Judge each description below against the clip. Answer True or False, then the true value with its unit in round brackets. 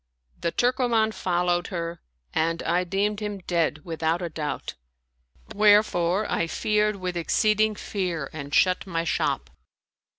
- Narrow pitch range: False (3.9 semitones)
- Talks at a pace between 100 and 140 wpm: True (135 wpm)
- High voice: False (180 Hz)